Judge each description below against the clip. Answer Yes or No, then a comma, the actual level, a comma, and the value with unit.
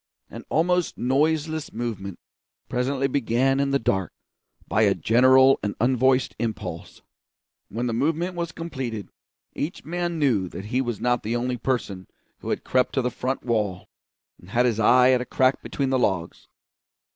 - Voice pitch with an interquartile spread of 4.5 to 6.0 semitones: No, average, 3.6 semitones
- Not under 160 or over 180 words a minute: Yes, average, 165 wpm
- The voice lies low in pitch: Yes, low, 125 Hz